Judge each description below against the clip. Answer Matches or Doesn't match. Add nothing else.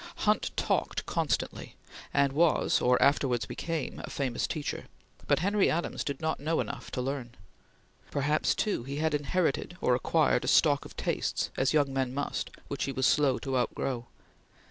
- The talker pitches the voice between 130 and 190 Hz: Matches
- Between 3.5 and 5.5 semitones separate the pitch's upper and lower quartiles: Doesn't match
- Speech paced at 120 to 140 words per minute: Doesn't match